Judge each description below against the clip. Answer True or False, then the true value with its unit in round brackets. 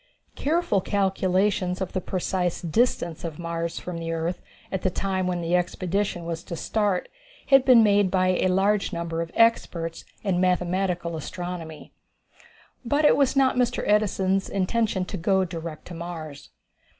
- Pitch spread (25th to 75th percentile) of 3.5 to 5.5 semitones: False (3.0 semitones)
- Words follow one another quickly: False (155 wpm)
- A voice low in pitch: False (185 Hz)